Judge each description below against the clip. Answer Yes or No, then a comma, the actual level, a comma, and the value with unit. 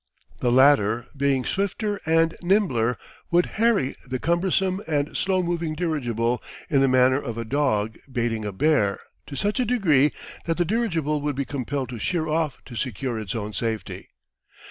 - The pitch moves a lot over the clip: Yes, wide, 6.1 semitones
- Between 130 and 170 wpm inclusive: Yes, average, 165 wpm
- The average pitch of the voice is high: No, medium, 140 Hz